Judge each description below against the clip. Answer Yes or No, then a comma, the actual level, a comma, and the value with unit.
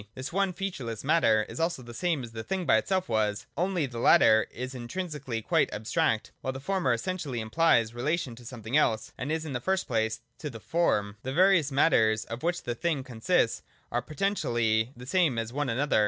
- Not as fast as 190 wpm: No, average, 200 wpm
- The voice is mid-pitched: No, low, 130 Hz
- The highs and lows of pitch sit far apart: Yes, wide, 6.5 semitones